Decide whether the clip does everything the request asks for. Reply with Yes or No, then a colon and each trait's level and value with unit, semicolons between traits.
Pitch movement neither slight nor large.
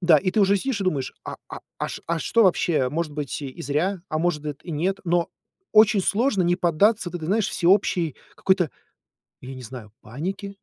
Yes: average, 4.6 semitones